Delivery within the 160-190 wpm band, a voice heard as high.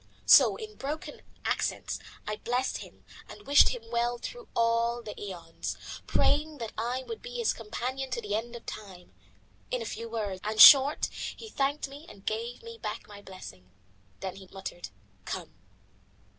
Yes: average, 165 wpm; high, 235 Hz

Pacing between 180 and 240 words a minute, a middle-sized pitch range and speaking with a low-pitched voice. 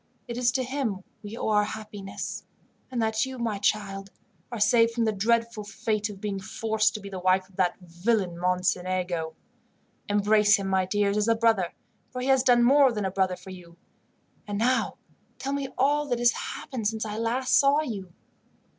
No: average, 190 wpm; average, 3.6 semitones; high, 215 Hz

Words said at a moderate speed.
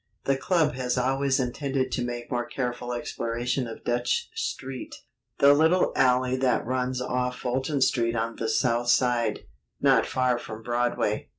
Yes: average, 155 wpm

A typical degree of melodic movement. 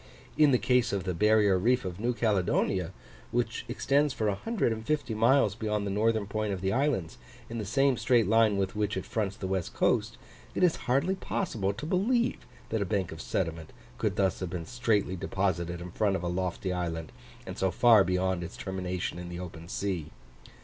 Yes: average, 4.2 semitones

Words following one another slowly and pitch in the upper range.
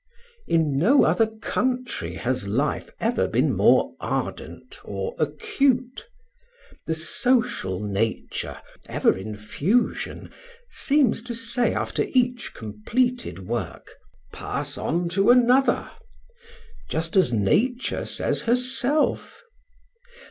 Yes: slow, 100 wpm; high, 230 Hz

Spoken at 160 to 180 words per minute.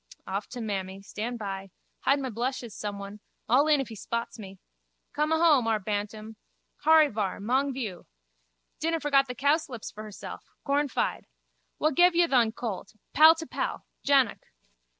No: average, 150 wpm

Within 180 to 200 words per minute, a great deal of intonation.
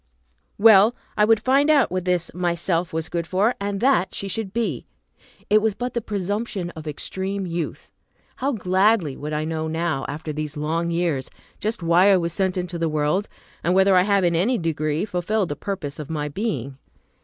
No: average, 190 wpm; average, 4.1 semitones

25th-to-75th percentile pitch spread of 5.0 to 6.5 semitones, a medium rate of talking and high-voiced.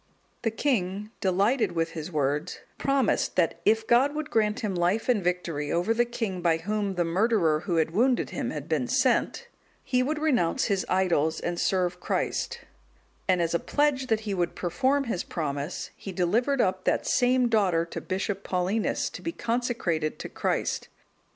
Yes: wide, 5.6 semitones; average, 175 wpm; high, 195 Hz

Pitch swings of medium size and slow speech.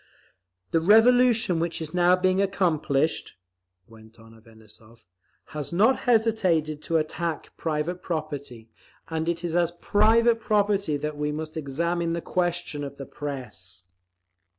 Yes: average, 4.2 semitones; slow, 130 wpm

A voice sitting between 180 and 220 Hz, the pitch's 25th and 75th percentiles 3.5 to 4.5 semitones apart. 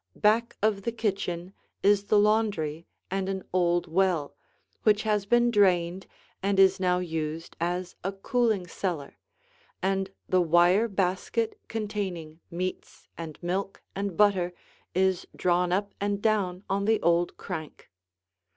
No: high, 190 Hz; average, 2.7 semitones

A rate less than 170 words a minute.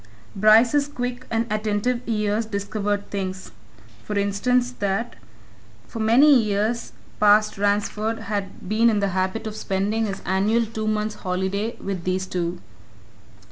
Yes: slow, 135 wpm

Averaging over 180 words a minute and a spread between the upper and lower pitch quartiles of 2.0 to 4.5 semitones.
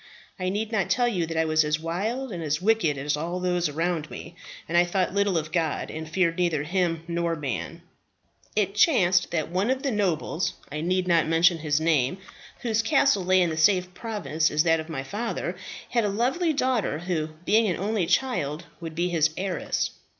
Yes: average, 200 wpm; average, 4.1 semitones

